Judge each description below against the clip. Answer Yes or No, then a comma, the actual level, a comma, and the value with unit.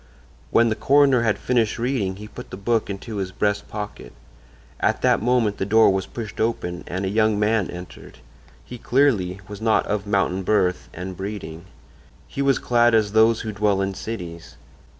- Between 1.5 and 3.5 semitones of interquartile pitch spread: Yes, average, 3.0 semitones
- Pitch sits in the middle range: No, low, 105 Hz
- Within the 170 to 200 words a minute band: Yes, average, 180 wpm